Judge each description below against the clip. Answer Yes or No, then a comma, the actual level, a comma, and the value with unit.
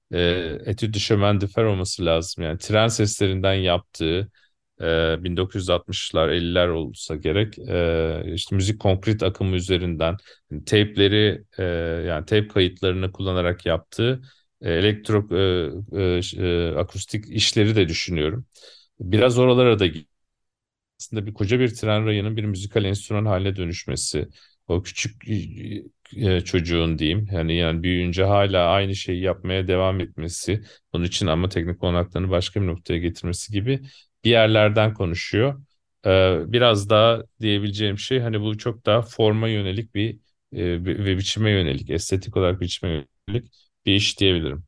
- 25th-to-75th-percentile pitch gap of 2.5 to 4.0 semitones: Yes, average, 3.5 semitones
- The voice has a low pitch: Yes, very low, 95 Hz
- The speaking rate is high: No, average, 125 wpm